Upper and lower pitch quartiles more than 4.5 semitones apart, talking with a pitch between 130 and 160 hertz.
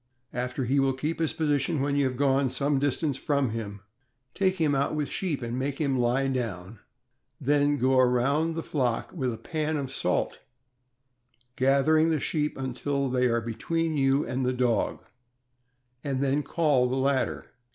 No: narrow, 2.6 semitones; low, 135 Hz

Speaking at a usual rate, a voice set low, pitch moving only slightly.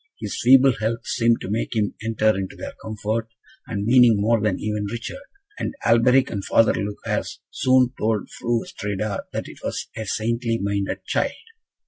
Yes: average, 165 wpm; low, 110 Hz; narrow, 2.2 semitones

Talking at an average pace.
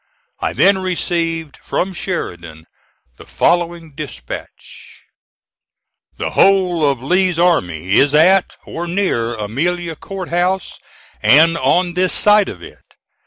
No: slow, 120 wpm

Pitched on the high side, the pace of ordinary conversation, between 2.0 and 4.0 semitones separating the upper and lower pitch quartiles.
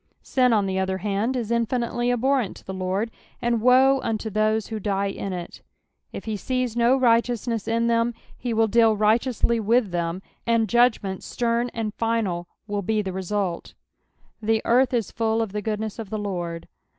Yes: high, 220 Hz; average, 185 wpm; average, 2.8 semitones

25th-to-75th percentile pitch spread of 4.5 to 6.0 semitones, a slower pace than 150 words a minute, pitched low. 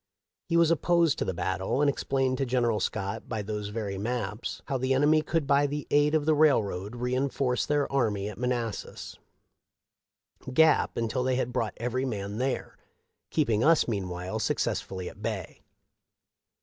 No: average, 5.1 semitones; average, 165 wpm; low, 125 Hz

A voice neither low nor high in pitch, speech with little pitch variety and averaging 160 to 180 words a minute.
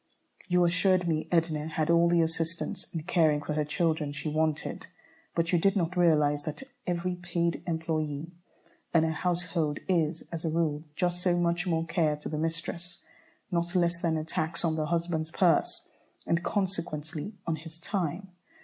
Yes: medium, 165 Hz; narrow, 1.9 semitones; average, 170 wpm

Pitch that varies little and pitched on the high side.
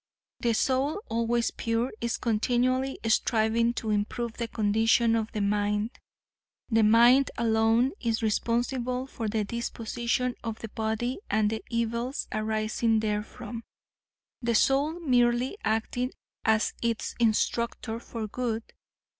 Yes: narrow, 1.6 semitones; high, 230 Hz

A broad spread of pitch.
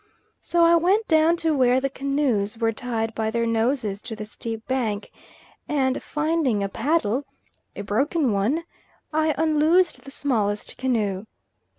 Yes: wide, 5.8 semitones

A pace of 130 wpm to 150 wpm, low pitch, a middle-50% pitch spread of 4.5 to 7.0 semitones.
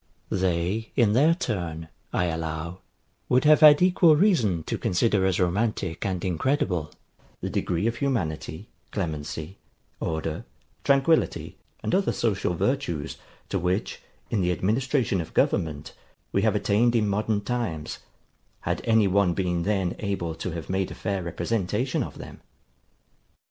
Yes: average, 140 wpm; very low, 95 Hz; wide, 5.6 semitones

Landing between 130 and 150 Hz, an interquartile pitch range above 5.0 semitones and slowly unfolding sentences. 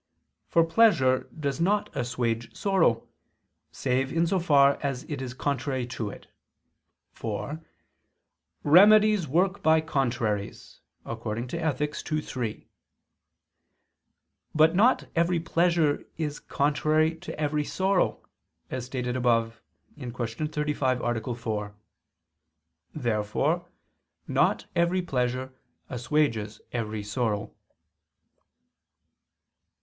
Yes: medium, 140 Hz; wide, 5.4 semitones; slow, 95 wpm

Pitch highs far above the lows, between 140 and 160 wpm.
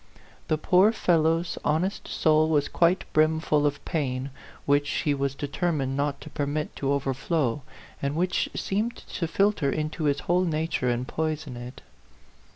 No: average, 2.9 semitones; average, 155 wpm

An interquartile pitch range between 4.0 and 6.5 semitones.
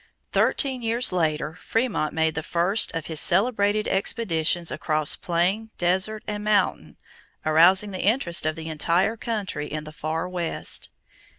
Yes: average, 4.8 semitones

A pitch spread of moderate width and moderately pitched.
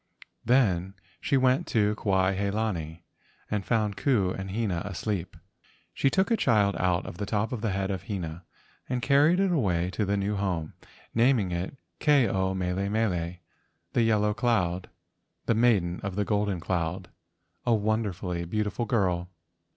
No: average, 3.7 semitones; low, 100 Hz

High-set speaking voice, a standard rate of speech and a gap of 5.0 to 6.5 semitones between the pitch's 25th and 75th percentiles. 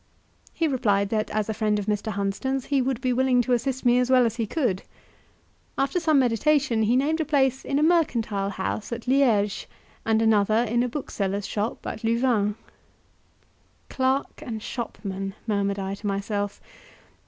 No: high, 230 Hz; average, 170 wpm; average, 4.2 semitones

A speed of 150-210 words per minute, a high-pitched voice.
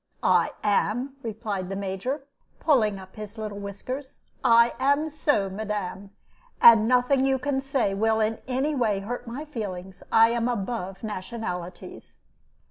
No: average, 140 wpm; high, 225 Hz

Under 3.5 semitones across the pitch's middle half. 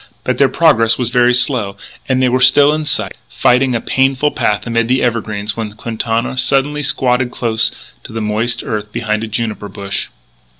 Yes: average, 2.9 semitones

